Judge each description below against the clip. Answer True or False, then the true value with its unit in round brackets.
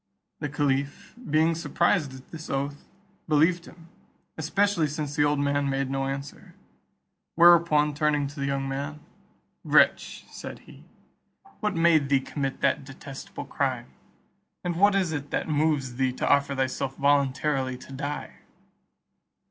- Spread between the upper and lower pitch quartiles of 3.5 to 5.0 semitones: False (2.6 semitones)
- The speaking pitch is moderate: True (145 Hz)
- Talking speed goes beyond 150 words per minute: False (140 wpm)